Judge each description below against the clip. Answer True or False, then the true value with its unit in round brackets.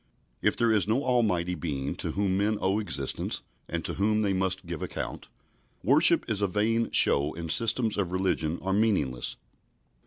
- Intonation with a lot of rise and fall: False (4.1 semitones)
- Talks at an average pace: True (175 wpm)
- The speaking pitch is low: True (95 Hz)